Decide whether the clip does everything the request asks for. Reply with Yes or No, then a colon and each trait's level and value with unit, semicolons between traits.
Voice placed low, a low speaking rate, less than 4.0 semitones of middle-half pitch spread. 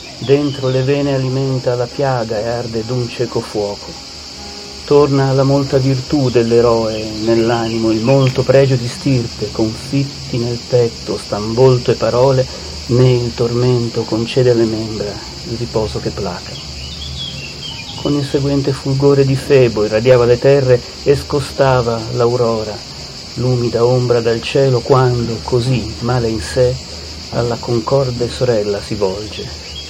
No: low, 120 Hz; average, 130 wpm; average, 2.9 semitones